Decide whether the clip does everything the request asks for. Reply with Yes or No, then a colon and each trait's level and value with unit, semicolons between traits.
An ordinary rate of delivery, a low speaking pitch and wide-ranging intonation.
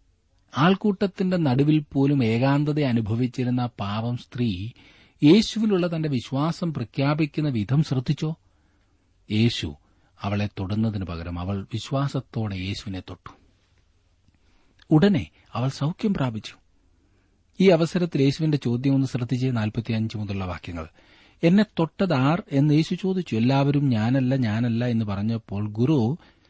Yes: average, 100 wpm; low, 120 Hz; wide, 6.9 semitones